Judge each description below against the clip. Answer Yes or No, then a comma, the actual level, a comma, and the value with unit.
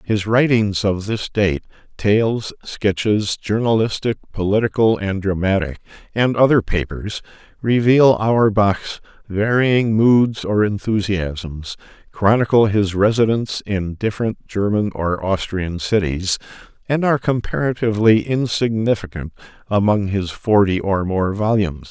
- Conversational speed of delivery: No, slow, 100 wpm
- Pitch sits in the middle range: No, low, 105 Hz